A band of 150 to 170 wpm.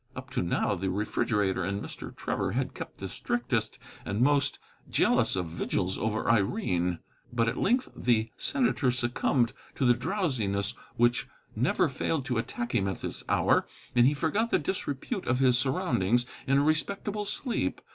Yes: average, 165 wpm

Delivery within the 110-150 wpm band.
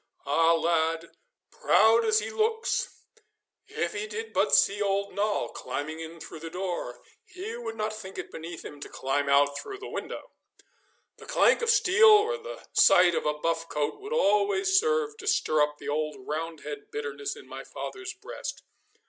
No: average, 175 wpm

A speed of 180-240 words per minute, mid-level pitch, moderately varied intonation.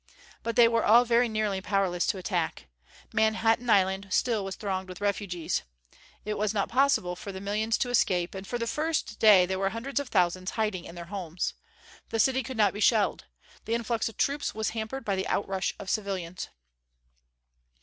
No: average, 190 wpm; high, 210 Hz; average, 3.3 semitones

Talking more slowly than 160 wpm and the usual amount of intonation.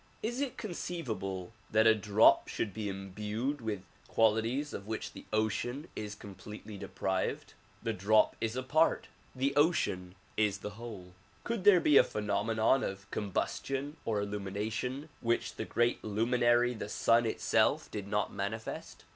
Yes: average, 145 wpm; average, 3.7 semitones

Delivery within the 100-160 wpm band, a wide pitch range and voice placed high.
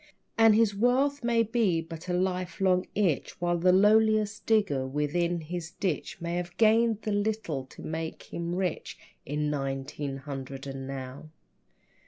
No: average, 150 wpm; wide, 6.1 semitones; medium, 175 Hz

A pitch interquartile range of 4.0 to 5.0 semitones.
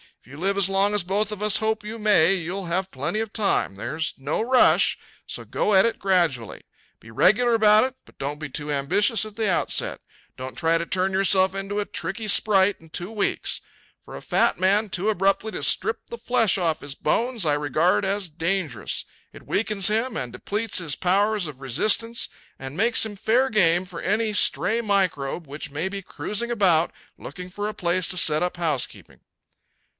Yes: average, 4.6 semitones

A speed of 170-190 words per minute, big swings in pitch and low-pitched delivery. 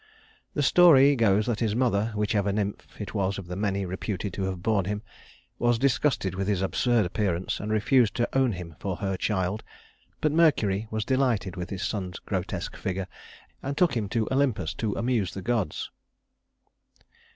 No: average, 175 wpm; average, 3.9 semitones; low, 105 Hz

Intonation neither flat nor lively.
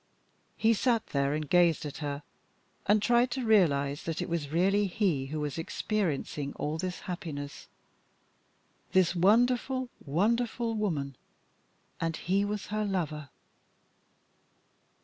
No: wide, 6.1 semitones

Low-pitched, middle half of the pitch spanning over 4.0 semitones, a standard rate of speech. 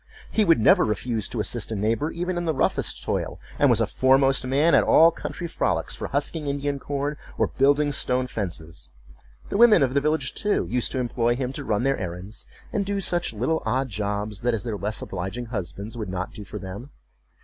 No: low, 125 Hz; wide, 5.5 semitones; fast, 210 wpm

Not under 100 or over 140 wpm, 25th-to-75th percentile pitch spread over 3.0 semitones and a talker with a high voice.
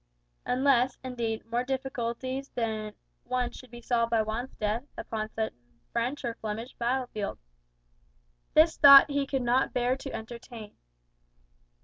No: slow, 135 wpm; narrow, 2.5 semitones; high, 240 Hz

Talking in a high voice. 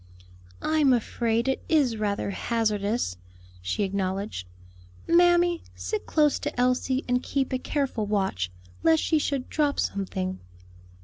Yes: high, 240 Hz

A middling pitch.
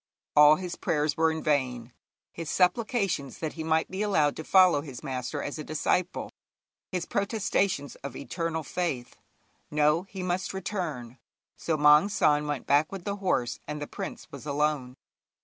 Yes: medium, 155 Hz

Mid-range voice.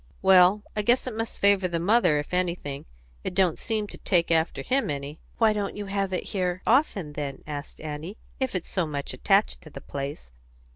Yes: medium, 180 Hz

